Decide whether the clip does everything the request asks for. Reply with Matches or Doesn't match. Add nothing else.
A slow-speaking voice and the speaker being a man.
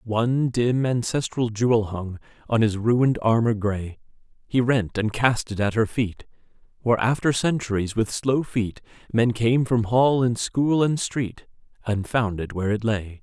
Doesn't match